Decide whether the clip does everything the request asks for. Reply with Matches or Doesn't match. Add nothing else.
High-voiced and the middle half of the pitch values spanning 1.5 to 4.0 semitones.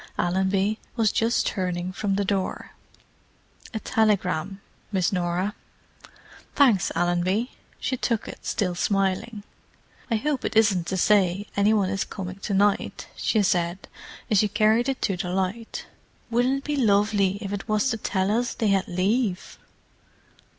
Matches